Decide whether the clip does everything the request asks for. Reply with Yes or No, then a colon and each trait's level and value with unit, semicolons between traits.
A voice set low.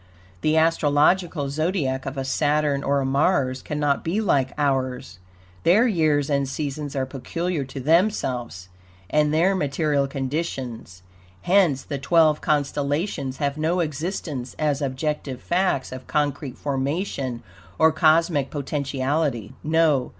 No: medium, 145 Hz